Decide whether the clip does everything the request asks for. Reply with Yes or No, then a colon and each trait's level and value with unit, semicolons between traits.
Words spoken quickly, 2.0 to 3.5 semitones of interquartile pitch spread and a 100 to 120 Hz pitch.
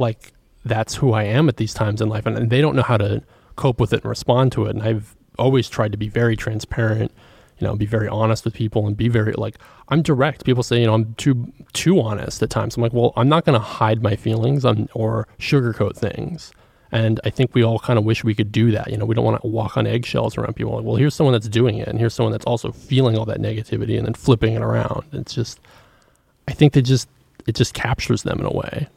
Yes: fast, 260 wpm; narrow, 2.6 semitones; low, 115 Hz